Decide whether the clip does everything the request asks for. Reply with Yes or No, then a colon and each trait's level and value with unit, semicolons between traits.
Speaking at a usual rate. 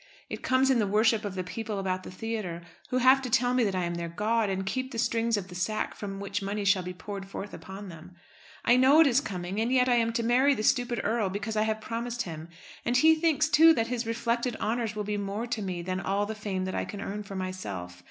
No: fast, 260 wpm